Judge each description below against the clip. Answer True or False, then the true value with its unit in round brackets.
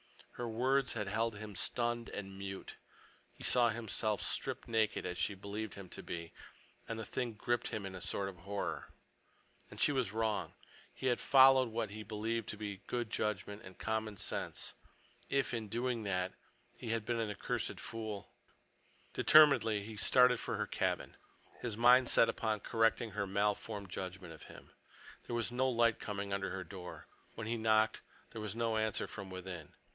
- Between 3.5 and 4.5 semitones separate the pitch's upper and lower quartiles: False (2.8 semitones)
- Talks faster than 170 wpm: True (180 wpm)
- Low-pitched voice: True (110 Hz)